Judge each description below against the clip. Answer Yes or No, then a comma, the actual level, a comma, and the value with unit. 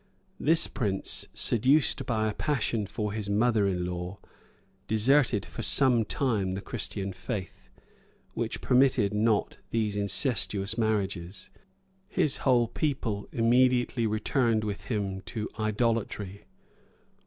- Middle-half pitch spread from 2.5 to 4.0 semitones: Yes, average, 3.3 semitones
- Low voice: Yes, low, 110 Hz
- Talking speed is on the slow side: Yes, slow, 115 wpm